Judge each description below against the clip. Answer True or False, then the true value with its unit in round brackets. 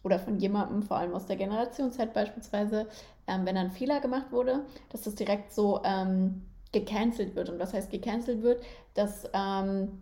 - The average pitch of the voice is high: True (205 Hz)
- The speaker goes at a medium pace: True (175 wpm)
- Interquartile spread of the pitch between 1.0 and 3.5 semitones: True (2.9 semitones)